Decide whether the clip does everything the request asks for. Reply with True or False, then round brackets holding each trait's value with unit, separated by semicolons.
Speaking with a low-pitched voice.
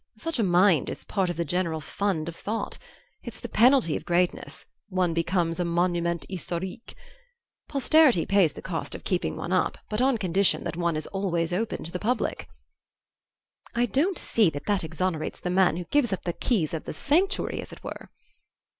False (180 Hz)